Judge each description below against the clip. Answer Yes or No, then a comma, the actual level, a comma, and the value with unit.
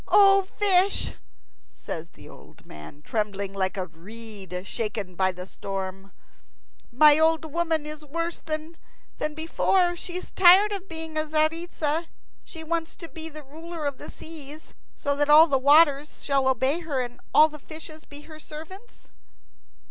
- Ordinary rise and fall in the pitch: No, wide, 5.7 semitones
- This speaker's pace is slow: No, average, 155 wpm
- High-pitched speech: Yes, very high, 305 Hz